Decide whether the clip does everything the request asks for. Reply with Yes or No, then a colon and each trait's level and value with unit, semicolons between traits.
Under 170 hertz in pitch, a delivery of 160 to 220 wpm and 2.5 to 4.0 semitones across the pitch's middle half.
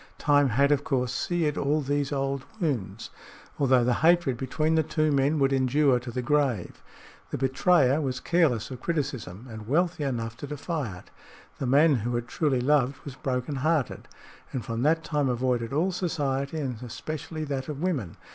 Yes: low, 135 Hz; average, 175 wpm; average, 3.4 semitones